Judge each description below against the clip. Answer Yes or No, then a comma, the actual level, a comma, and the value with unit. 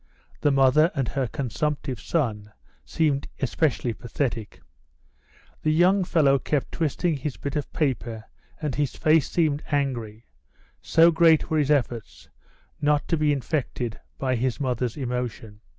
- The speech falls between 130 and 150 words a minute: Yes, slow, 135 wpm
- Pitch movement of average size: Yes, average, 3.8 semitones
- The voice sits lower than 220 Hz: Yes, medium, 140 Hz